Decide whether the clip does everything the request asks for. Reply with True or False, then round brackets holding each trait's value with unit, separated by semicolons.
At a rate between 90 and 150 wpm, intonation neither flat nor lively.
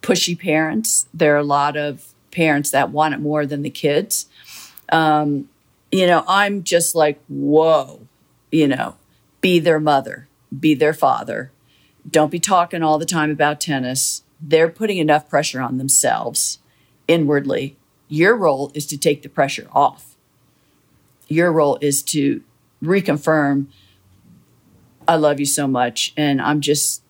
False (145 wpm; 2.3 semitones)